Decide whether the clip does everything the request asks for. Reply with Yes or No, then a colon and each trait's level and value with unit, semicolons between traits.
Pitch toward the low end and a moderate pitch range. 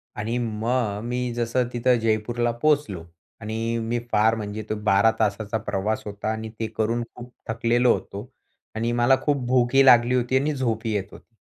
No: low, 115 Hz; narrow, 2.1 semitones